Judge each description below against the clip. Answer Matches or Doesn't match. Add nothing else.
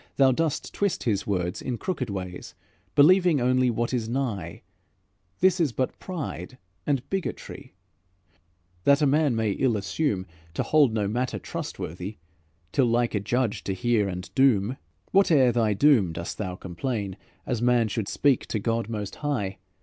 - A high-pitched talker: Doesn't match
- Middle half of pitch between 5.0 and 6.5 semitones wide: Matches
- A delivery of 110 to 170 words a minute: Matches